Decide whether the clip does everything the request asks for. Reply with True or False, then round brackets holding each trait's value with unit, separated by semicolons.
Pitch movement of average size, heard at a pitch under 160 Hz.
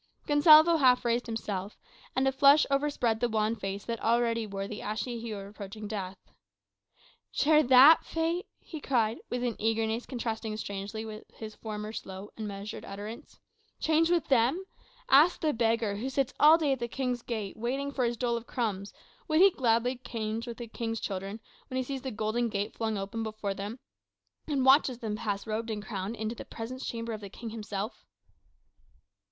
False (3.3 semitones; 230 Hz)